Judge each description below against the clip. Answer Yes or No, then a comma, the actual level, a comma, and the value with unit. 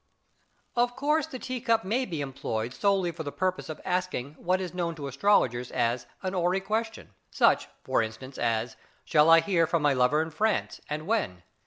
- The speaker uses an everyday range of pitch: No, wide, 6.9 semitones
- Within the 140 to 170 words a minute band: No, average, 190 wpm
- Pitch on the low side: No, medium, 170 Hz